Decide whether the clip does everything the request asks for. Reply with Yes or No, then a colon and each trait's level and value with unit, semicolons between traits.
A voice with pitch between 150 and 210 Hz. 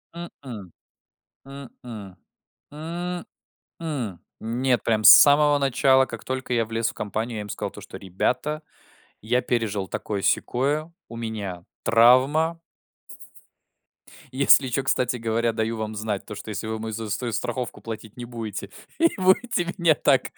No: low, 115 Hz